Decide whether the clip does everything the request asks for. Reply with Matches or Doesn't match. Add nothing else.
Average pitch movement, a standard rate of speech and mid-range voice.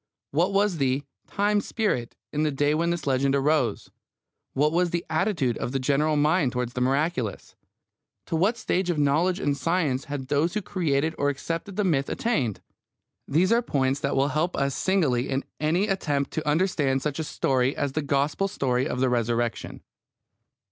Matches